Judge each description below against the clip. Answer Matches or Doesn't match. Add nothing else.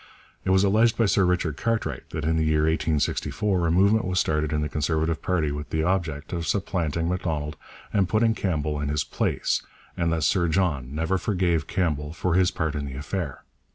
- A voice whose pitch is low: Matches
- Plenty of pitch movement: Doesn't match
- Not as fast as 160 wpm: Doesn't match